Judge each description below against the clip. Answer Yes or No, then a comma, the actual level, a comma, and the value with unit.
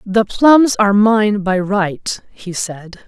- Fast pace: No, average, 155 wpm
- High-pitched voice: Yes, high, 210 Hz